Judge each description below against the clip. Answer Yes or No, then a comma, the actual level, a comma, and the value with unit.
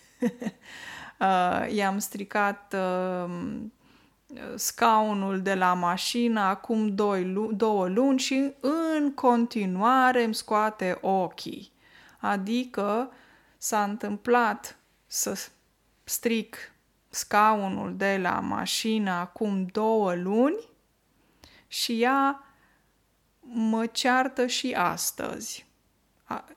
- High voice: Yes, high, 220 Hz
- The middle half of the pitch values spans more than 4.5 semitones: No, average, 3.9 semitones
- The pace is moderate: No, slow, 85 wpm